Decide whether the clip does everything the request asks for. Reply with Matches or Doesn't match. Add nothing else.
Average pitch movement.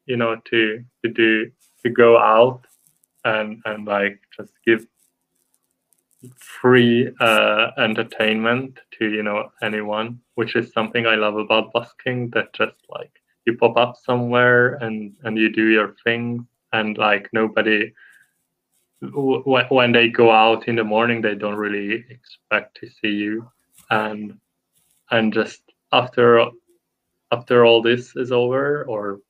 Doesn't match